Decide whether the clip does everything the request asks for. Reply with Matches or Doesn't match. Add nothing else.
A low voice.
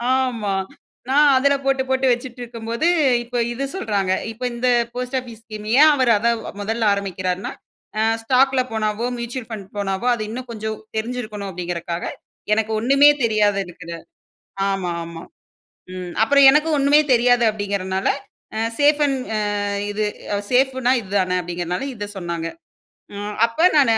Doesn't match